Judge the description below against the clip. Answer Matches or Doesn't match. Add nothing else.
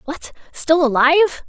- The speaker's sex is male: Doesn't match